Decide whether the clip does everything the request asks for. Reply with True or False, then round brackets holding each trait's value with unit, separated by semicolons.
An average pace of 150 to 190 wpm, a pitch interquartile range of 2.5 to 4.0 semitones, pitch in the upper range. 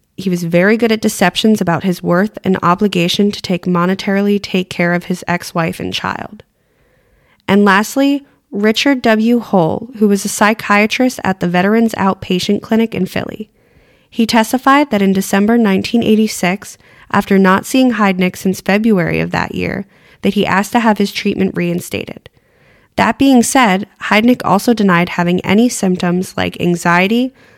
True (155 wpm; 3.4 semitones; 200 Hz)